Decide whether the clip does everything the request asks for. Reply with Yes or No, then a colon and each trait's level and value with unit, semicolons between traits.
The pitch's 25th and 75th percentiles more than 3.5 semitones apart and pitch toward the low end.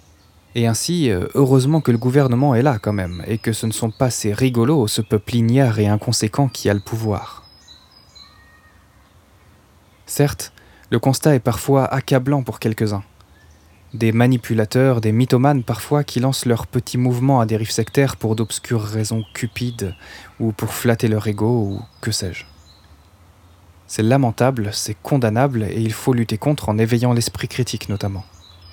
Yes: average, 4.0 semitones; low, 110 Hz